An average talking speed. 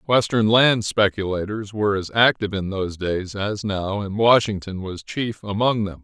Yes: average, 170 wpm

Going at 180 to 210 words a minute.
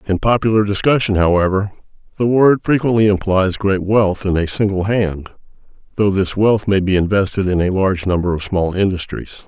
No: average, 170 wpm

